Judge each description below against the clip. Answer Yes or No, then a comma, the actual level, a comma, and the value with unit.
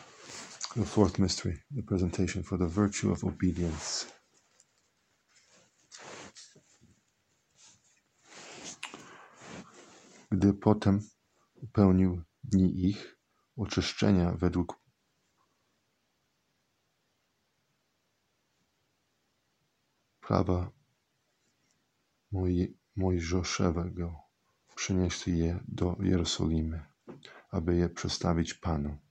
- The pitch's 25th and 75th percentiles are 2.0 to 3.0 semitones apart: Yes, narrow, 2.4 semitones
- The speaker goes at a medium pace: No, slow, 55 wpm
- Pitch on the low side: Yes, very low, 90 Hz